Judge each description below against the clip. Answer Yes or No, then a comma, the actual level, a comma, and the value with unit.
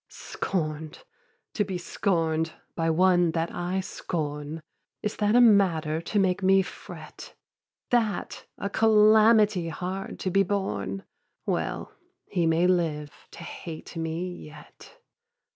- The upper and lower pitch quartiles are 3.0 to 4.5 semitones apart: Yes, average, 3.6 semitones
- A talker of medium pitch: Yes, medium, 180 Hz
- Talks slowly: Yes, slow, 125 wpm